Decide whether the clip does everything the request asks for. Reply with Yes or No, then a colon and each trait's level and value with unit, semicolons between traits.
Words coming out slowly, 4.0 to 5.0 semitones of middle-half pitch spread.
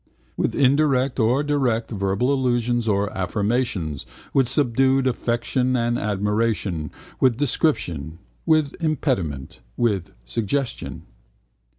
Yes: slow, 95 wpm; average, 4.6 semitones